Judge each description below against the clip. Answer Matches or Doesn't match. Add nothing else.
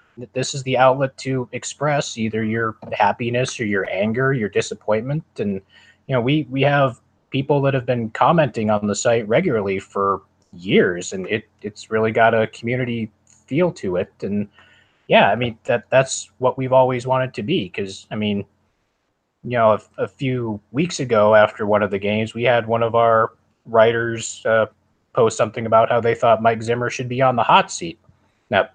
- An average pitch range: Matches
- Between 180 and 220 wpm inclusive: Matches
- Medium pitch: Doesn't match